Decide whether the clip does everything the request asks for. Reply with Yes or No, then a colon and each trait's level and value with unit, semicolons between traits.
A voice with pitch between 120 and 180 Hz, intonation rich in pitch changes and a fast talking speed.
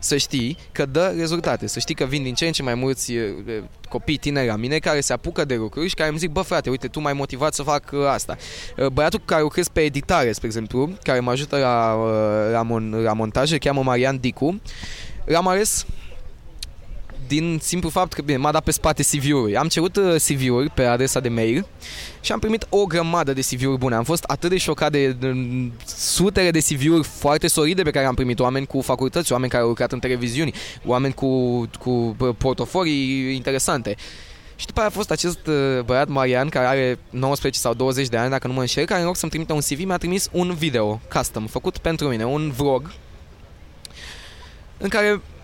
No: low, 135 Hz; average, 4.4 semitones; fast, 200 wpm